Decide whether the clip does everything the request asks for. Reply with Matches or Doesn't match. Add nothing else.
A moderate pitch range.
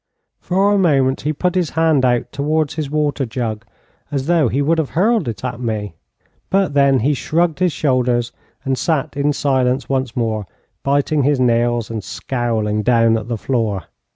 Matches